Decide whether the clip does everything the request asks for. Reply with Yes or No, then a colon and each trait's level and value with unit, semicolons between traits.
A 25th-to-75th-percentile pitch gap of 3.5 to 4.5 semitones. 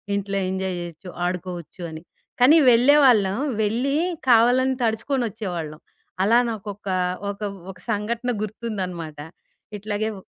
Yes: average, 4.0 semitones